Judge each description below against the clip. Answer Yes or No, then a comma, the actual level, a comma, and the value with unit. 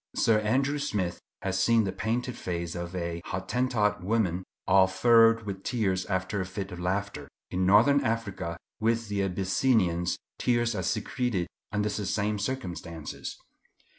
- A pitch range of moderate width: Yes, average, 3.7 semitones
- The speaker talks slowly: No, average, 145 wpm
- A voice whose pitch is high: No, low, 100 Hz